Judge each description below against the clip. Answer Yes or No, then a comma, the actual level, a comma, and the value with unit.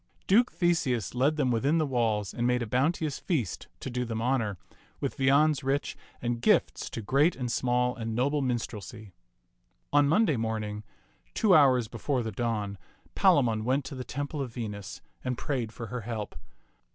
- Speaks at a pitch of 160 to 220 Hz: No, low, 125 Hz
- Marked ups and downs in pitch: No, average, 3.8 semitones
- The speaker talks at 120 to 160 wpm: No, average, 170 wpm